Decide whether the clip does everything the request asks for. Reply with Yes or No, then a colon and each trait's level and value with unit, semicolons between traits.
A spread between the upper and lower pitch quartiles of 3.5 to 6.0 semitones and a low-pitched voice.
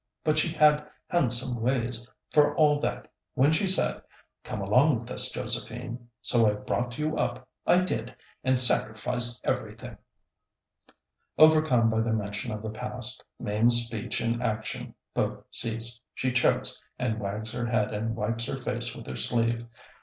No: narrow, 2.6 semitones; low, 120 Hz